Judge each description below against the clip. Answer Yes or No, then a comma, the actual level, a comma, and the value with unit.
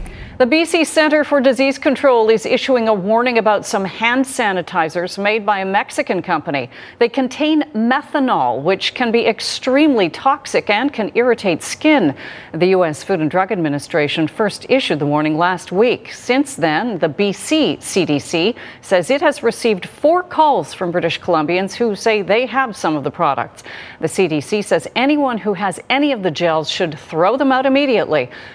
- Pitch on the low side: No, high, 225 Hz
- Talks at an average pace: Yes, average, 170 wpm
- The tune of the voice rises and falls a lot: Yes, wide, 6.8 semitones